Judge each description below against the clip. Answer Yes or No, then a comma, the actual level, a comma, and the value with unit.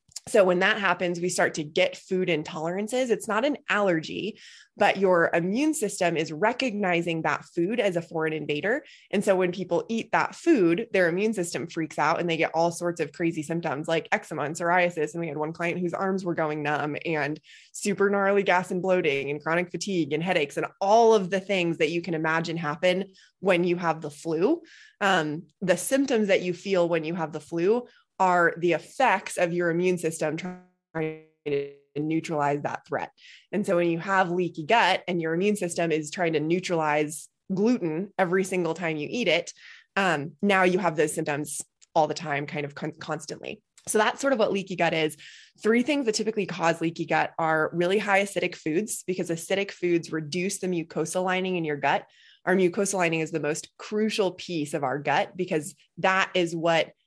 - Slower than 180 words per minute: No, average, 200 wpm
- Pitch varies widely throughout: No, average, 3.2 semitones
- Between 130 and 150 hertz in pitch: No, medium, 175 Hz